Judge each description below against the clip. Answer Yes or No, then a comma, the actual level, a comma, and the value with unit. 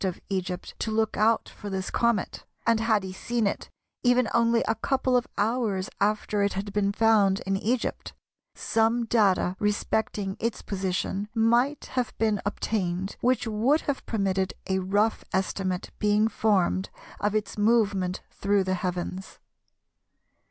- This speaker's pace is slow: No, average, 145 wpm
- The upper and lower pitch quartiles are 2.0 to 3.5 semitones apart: Yes, average, 2.9 semitones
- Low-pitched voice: No, high, 210 Hz